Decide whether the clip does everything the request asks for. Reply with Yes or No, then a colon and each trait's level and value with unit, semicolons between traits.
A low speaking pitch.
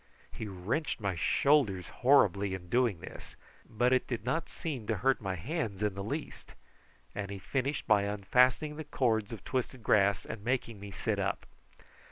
Yes: low, 110 Hz